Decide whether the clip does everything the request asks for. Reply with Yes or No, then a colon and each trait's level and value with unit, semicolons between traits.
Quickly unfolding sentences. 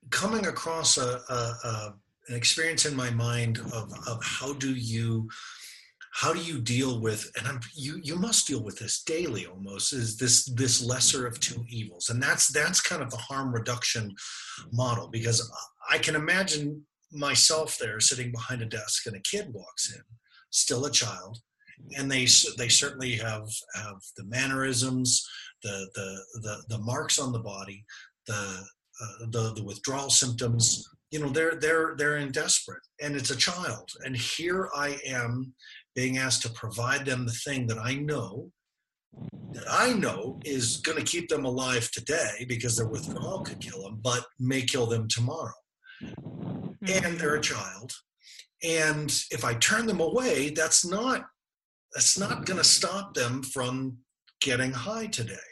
No: average, 165 wpm